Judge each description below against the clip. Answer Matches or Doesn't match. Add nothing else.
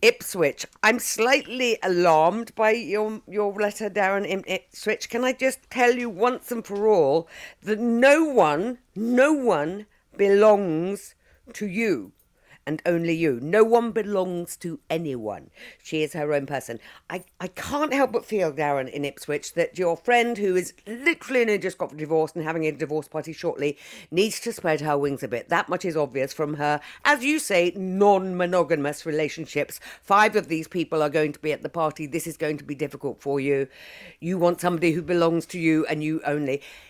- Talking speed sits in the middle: Matches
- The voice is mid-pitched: Matches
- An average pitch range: Doesn't match